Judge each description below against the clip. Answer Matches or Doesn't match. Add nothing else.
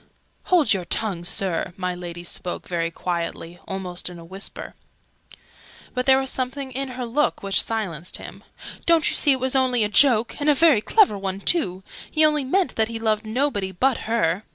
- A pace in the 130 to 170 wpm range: Doesn't match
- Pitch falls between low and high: Doesn't match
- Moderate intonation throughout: Doesn't match